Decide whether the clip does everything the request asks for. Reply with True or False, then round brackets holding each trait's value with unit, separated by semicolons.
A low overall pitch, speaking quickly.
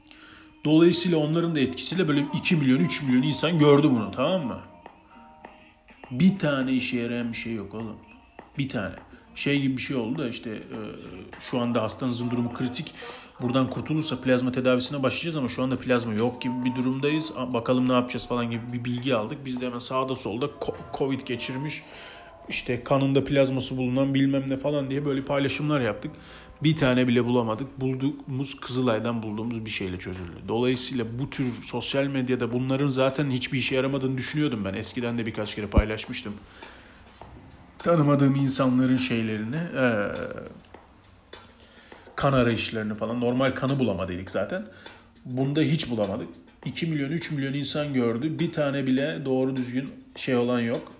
True (130 Hz; 150 wpm)